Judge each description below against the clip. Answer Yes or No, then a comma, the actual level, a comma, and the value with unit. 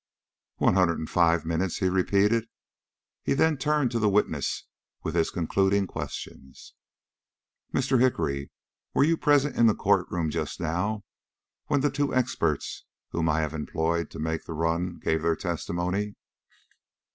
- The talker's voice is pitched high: No, very low, 90 Hz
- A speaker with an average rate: Yes, average, 150 wpm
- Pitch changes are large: Yes, wide, 5.9 semitones